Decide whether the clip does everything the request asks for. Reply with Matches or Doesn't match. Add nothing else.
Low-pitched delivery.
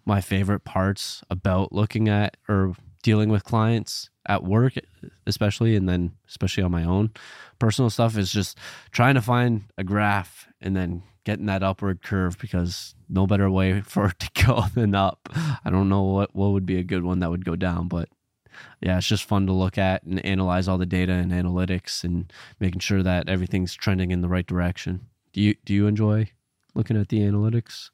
Matches